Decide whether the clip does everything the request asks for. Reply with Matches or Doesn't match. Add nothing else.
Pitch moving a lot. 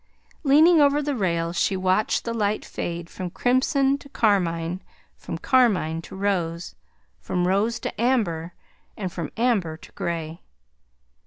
Matches